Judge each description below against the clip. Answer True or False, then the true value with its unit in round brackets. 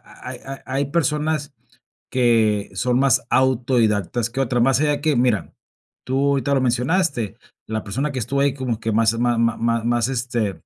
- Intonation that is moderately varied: True (3.0 semitones)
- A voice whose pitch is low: True (125 Hz)